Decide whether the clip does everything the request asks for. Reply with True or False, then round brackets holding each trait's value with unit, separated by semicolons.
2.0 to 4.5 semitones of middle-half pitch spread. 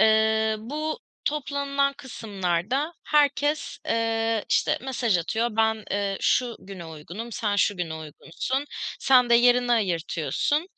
False (5.0 semitones)